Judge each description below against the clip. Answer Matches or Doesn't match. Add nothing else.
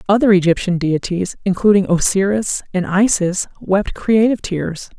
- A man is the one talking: Doesn't match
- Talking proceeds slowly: Matches